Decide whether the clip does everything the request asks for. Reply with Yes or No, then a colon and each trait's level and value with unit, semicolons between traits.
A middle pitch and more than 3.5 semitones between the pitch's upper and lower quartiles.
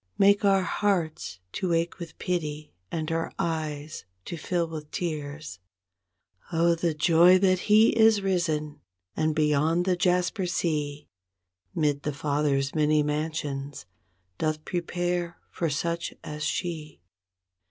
No: medium, 160 Hz; average, 2.8 semitones